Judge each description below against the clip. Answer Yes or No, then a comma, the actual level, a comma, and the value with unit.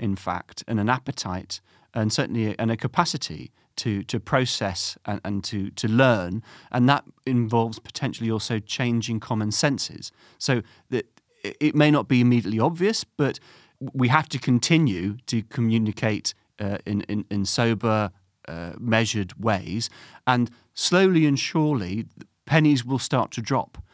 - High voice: No, low, 115 Hz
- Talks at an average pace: Yes, average, 150 wpm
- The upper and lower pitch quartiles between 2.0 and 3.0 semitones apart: No, average, 4.1 semitones